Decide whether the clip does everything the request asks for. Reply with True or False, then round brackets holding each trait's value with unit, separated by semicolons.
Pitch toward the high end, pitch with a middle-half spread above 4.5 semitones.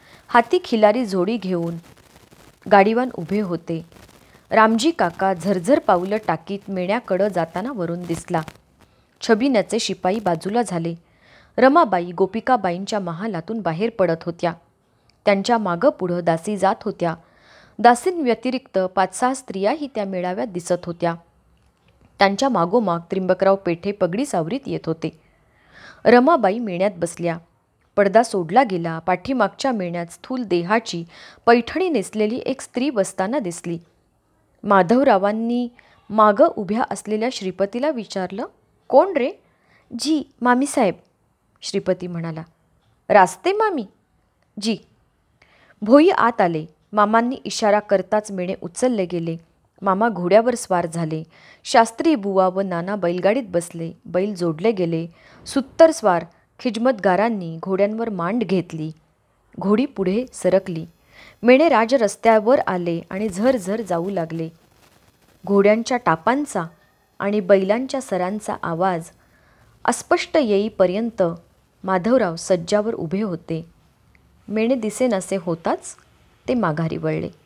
True (195 Hz; 5.2 semitones)